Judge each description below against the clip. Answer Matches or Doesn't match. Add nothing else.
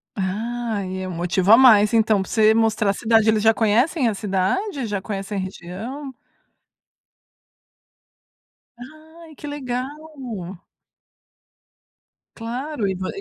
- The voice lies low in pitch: Doesn't match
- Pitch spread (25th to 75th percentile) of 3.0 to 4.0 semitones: Doesn't match